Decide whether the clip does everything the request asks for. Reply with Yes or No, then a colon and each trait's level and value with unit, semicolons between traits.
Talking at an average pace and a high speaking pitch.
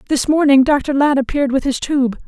No: fast, 210 wpm; very high, 275 Hz